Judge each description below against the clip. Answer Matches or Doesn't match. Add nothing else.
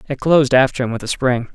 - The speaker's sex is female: Doesn't match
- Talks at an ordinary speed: Doesn't match